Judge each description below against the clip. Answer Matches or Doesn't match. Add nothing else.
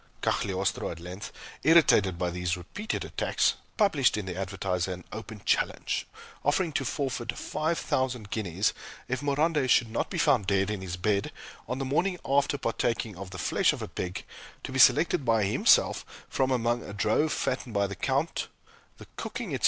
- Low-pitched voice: Matches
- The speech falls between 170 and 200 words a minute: Matches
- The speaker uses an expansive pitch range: Matches